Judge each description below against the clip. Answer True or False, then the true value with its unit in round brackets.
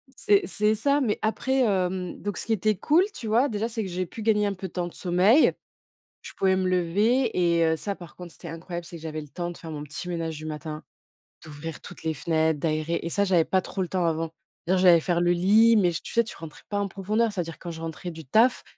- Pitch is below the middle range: False (180 Hz)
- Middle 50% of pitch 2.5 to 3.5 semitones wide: False (4.2 semitones)